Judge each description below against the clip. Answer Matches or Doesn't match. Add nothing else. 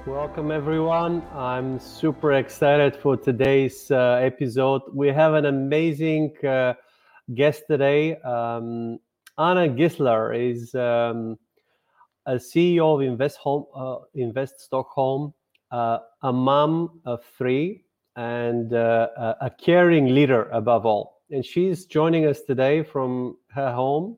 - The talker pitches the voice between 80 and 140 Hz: Matches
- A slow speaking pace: Matches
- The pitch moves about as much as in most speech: Matches